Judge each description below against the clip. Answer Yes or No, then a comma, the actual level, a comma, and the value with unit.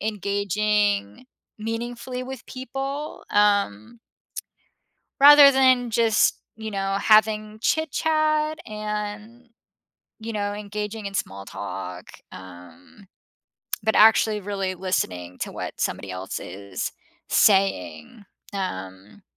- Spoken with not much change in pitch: No, average, 4.1 semitones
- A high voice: Yes, high, 210 Hz